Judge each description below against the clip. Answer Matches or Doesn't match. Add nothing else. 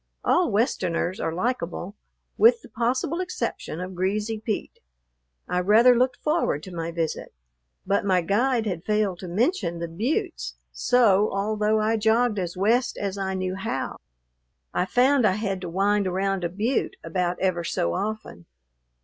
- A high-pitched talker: Matches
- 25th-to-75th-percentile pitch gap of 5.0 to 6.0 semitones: Doesn't match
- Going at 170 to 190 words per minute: Doesn't match